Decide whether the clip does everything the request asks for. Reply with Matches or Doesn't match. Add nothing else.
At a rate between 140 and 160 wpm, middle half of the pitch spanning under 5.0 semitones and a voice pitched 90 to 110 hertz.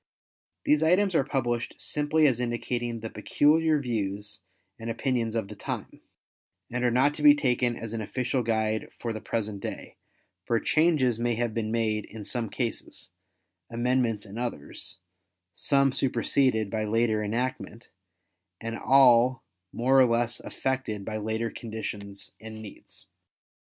Doesn't match